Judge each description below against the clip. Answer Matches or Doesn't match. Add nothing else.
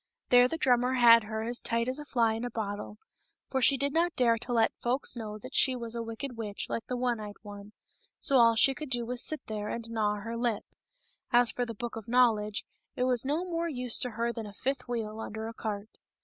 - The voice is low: Doesn't match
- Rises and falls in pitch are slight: Matches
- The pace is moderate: Doesn't match